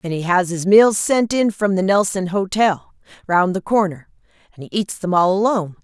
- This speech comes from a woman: Yes, female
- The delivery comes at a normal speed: Yes, average, 195 wpm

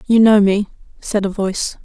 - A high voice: Yes, high, 205 Hz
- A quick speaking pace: No, average, 195 wpm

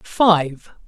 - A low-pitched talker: No, medium, 175 Hz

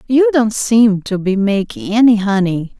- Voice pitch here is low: No, high, 215 Hz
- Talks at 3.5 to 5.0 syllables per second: Yes, 4.2 syllables/s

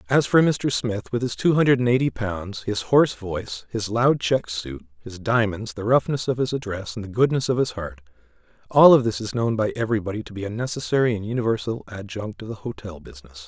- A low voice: Yes, low, 110 Hz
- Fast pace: Yes, fast, 215 wpm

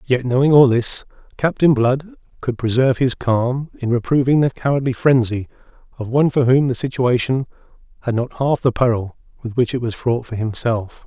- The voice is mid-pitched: No, low, 125 Hz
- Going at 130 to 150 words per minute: No, average, 180 wpm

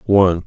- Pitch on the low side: Yes, very low, 95 Hz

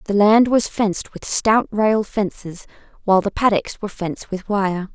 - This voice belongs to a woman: Yes, female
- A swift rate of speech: No, average, 180 wpm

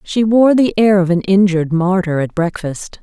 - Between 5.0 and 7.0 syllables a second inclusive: No, 4.8 syllables/s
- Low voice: No, high, 190 Hz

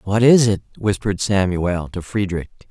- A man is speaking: Yes, male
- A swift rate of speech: No, average, 155 wpm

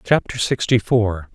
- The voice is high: No, low, 110 Hz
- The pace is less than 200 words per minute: Yes, slow, 135 wpm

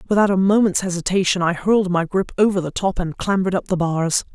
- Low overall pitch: No, medium, 185 Hz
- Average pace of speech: No, fast, 220 wpm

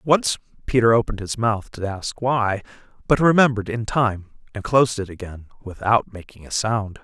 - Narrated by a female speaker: No, male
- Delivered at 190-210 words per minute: No, average, 170 wpm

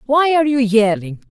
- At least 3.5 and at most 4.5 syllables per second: No, 5.3 syllables/s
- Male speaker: No, female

